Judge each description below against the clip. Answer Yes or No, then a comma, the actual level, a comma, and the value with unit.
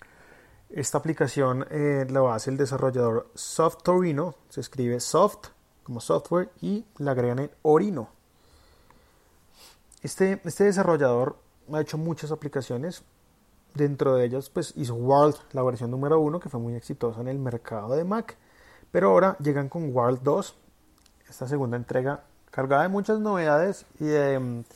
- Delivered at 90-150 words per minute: Yes, average, 145 wpm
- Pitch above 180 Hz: No, medium, 145 Hz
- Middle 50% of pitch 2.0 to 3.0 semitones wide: No, average, 4.1 semitones